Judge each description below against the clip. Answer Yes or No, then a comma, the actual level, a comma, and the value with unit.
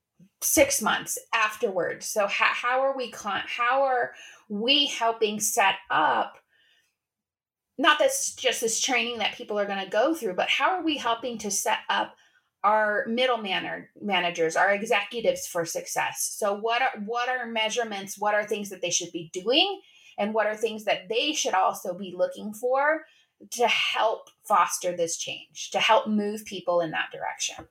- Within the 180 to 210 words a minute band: No, average, 170 wpm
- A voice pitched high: Yes, high, 220 Hz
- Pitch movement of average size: Yes, average, 4.6 semitones